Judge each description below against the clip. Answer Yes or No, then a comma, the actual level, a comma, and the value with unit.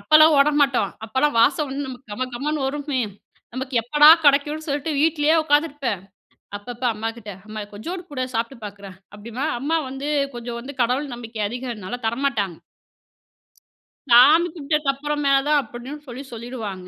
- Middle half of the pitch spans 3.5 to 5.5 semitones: Yes, average, 4.0 semitones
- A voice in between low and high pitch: No, very high, 260 Hz